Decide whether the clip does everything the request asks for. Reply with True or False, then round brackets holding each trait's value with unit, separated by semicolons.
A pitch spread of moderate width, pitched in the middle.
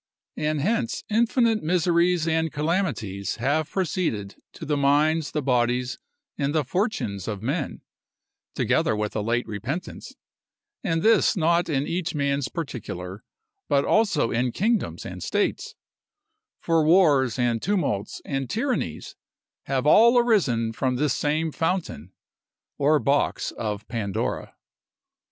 False (6.4 semitones; 150 Hz)